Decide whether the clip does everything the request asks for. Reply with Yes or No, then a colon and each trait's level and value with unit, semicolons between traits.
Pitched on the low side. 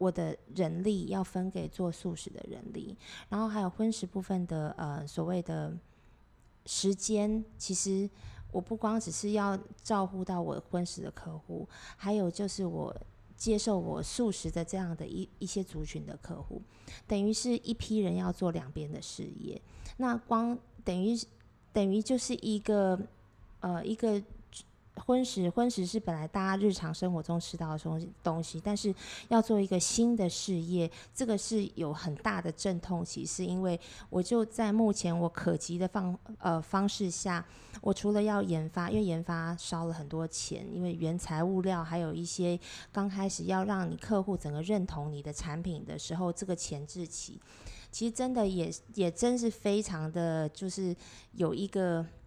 No: medium, 185 Hz